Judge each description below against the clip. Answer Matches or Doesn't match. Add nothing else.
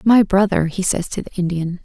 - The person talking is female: Matches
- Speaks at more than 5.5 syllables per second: Doesn't match